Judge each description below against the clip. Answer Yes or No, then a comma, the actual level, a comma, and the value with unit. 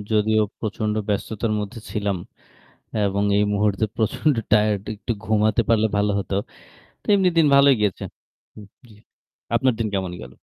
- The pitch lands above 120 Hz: No, low, 105 Hz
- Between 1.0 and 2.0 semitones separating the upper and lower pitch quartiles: Yes, narrow, 1.5 semitones